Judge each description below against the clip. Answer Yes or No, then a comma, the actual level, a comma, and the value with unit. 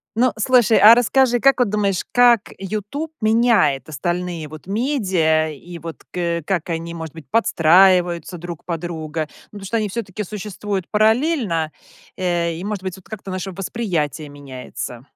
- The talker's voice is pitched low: No, medium, 185 Hz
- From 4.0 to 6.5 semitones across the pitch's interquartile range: Yes, average, 4.6 semitones